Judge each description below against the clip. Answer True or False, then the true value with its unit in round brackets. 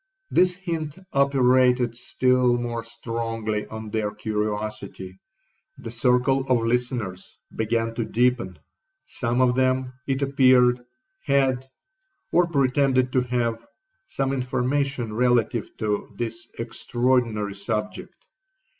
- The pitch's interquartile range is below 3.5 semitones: True (2.5 semitones)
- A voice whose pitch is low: True (125 Hz)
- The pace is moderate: False (100 wpm)